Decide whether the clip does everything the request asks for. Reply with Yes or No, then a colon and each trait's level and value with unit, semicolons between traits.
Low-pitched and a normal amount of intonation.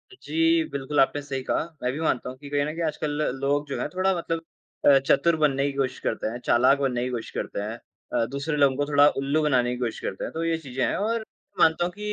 No: medium, 145 Hz; average, 3.5 semitones